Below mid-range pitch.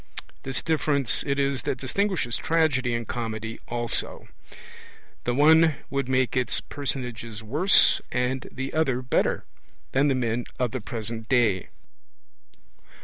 Yes: low, 130 Hz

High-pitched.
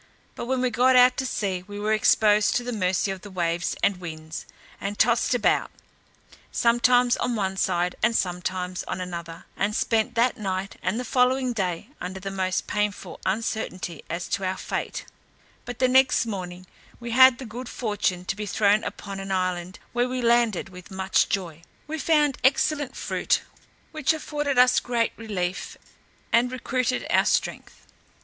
Yes: high, 210 Hz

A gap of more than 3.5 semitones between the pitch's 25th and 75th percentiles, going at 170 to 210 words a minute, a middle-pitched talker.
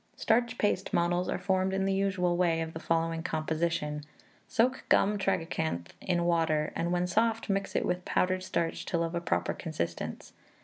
No: average, 2.8 semitones; average, 175 wpm; medium, 175 Hz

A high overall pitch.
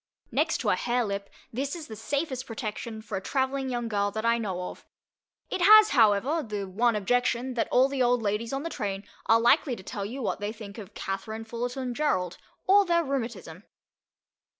Yes: high, 235 Hz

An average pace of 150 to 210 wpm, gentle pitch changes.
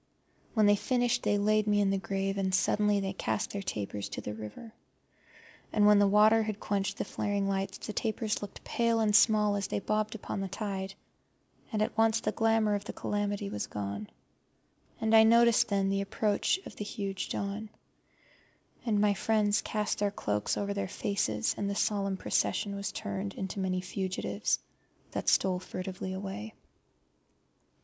Yes: average, 175 wpm; narrow, 1.8 semitones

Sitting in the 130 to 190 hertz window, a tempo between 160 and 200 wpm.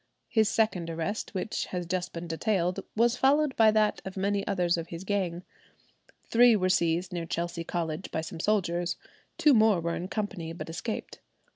Yes: medium, 185 Hz; average, 175 wpm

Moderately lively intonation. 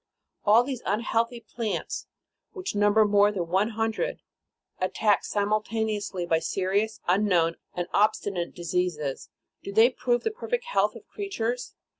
Yes: average, 3.7 semitones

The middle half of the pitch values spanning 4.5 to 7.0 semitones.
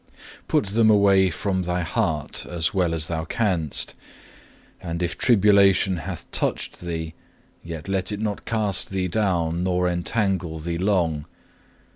No: average, 2.9 semitones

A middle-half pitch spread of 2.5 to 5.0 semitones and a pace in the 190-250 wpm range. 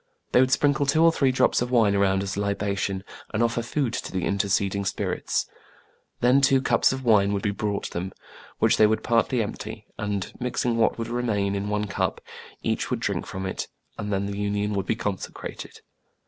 Yes: average, 3.4 semitones; average, 200 wpm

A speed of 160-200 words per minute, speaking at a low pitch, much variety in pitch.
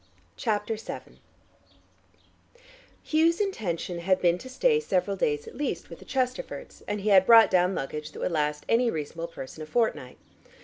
No: average, 170 wpm; high, 190 Hz; wide, 6.6 semitones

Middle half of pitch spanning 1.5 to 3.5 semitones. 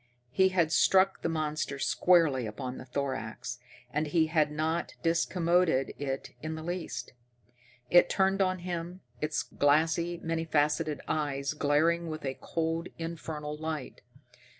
Yes: narrow, 2.6 semitones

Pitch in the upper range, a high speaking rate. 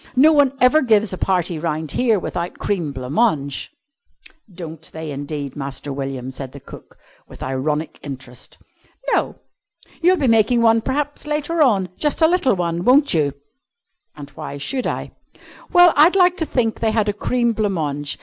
No: high, 195 Hz; average, 170 wpm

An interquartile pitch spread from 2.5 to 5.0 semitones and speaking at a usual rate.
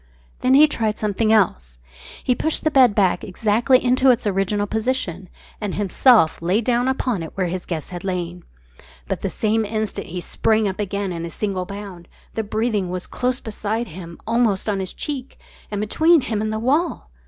Yes: average, 4.4 semitones; average, 190 wpm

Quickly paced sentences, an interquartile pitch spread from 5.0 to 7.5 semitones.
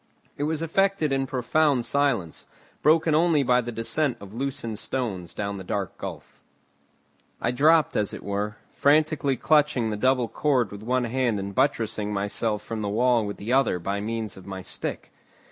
No: average, 175 wpm; wide, 5.4 semitones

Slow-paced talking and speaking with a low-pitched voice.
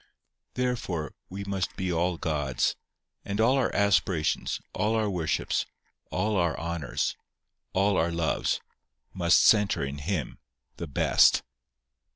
Yes: slow, 125 wpm; very low, 90 Hz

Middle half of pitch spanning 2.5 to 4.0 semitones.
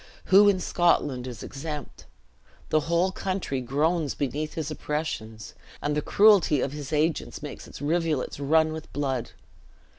Yes: average, 3.1 semitones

